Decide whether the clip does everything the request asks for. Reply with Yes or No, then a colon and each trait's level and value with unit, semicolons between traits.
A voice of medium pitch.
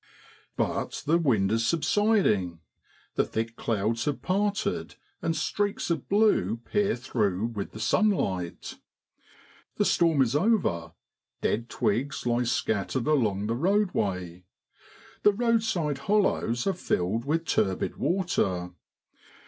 No: low, 125 Hz